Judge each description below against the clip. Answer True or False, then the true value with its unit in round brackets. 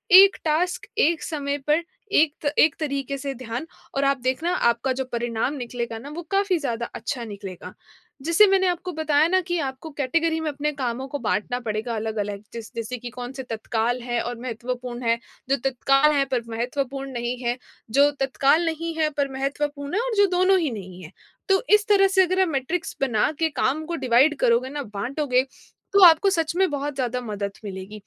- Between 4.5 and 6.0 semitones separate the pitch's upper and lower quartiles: True (5.0 semitones)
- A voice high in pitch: True (275 Hz)